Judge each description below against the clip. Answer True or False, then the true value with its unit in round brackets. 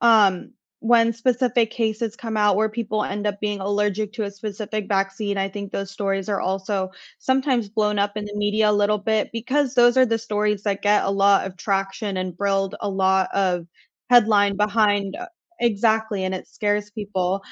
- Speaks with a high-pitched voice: True (205 Hz)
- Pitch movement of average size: False (2.0 semitones)